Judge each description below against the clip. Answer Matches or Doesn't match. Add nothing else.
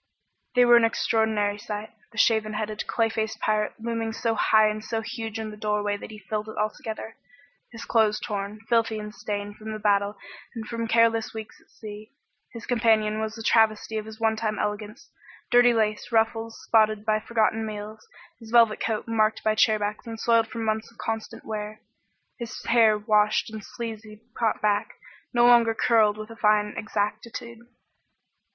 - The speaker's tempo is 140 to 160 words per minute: Doesn't match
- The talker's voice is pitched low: Doesn't match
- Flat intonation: Matches